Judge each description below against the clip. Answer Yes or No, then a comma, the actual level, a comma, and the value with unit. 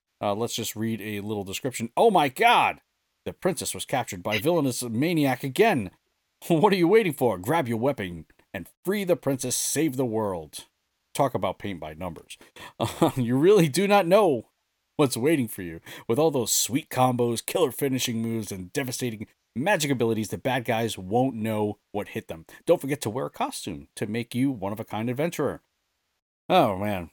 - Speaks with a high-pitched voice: No, low, 120 Hz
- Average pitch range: Yes, average, 4.8 semitones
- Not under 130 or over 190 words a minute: Yes, average, 185 wpm